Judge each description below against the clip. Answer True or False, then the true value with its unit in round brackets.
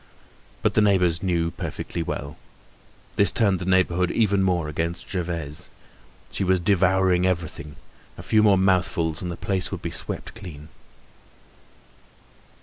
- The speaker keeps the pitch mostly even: True (2.2 semitones)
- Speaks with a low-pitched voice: True (90 Hz)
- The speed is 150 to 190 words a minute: False (140 wpm)